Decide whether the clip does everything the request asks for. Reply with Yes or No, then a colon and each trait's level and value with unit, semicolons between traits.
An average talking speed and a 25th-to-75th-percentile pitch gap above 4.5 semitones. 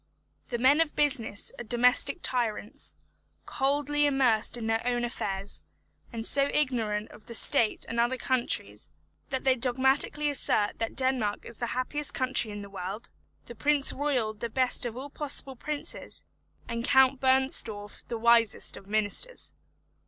No: average, 150 wpm; average, 3.4 semitones